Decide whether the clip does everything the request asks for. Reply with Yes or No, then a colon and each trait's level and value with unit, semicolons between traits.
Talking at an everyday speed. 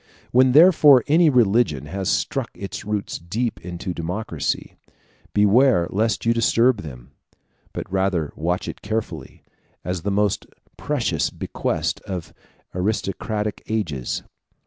No: slow, 125 wpm